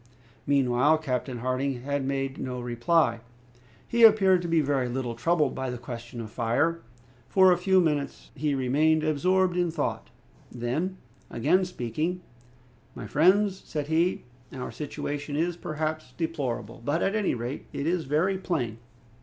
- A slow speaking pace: No, average, 150 wpm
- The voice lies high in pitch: No, medium, 145 Hz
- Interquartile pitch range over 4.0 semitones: Yes, wide, 5.4 semitones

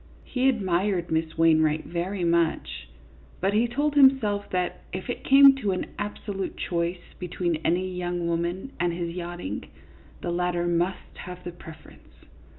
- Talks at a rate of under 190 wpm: Yes, average, 150 wpm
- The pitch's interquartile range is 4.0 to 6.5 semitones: No, average, 2.9 semitones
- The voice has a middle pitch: Yes, medium, 180 Hz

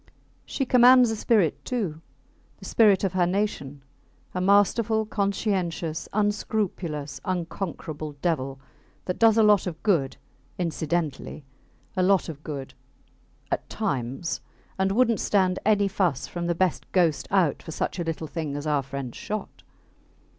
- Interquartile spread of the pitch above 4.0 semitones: Yes, average, 5.0 semitones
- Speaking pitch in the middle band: Yes, medium, 180 Hz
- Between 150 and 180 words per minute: No, average, 140 wpm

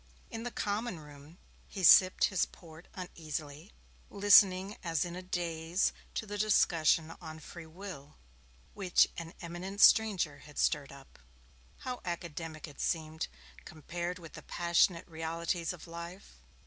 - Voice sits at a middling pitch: Yes, medium, 170 Hz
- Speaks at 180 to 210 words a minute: No, slow, 135 wpm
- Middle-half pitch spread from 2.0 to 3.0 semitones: Yes, average, 2.7 semitones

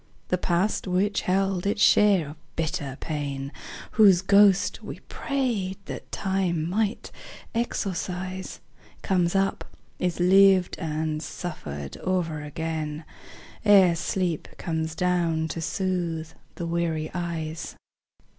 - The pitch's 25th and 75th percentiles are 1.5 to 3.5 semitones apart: Yes, average, 3.2 semitones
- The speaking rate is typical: No, slow, 110 wpm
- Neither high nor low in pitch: Yes, medium, 175 Hz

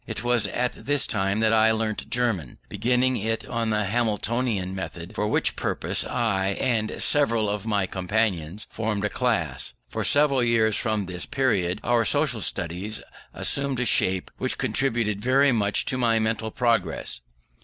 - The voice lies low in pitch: Yes, low, 110 Hz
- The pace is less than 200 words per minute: Yes, average, 160 wpm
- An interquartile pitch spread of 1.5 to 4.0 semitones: Yes, average, 3.1 semitones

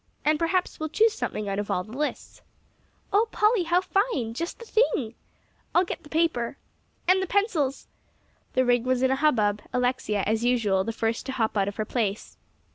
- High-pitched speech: Yes, very high, 255 Hz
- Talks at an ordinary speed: Yes, average, 195 wpm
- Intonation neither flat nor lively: No, wide, 7.5 semitones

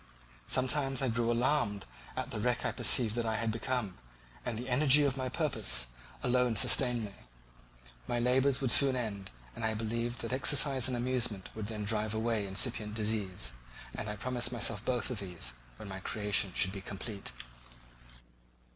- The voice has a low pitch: Yes, low, 115 Hz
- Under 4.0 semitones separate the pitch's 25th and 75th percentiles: Yes, average, 3.4 semitones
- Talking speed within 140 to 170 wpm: Yes, average, 165 wpm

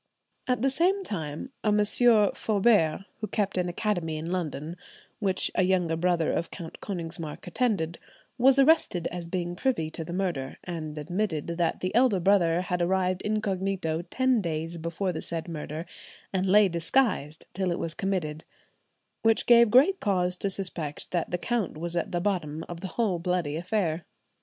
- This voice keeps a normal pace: Yes, average, 170 wpm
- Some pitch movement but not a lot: Yes, average, 4.0 semitones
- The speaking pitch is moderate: Yes, medium, 180 Hz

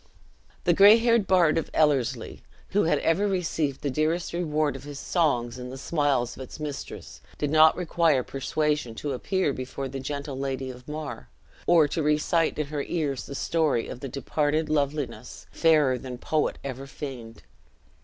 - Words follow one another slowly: No, average, 170 wpm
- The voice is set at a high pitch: No, medium, 150 Hz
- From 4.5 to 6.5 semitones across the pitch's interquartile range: No, average, 3.2 semitones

